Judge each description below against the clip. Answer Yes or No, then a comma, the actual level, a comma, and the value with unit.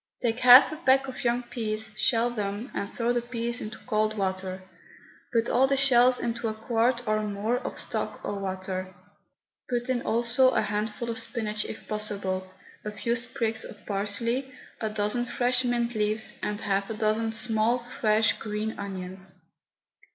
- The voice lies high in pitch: Yes, high, 220 Hz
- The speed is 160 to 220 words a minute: Yes, average, 165 wpm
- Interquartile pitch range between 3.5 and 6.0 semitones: No, narrow, 2.5 semitones